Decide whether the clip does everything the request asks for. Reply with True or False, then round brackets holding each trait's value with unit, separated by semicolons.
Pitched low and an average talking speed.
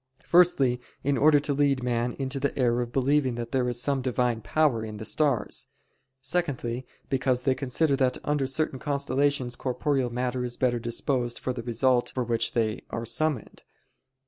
True (130 Hz; 170 wpm)